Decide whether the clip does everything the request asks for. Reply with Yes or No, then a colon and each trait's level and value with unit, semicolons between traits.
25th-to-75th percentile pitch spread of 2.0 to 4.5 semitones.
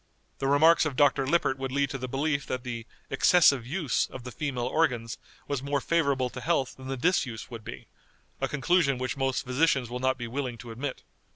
Yes: narrow, 2.4 semitones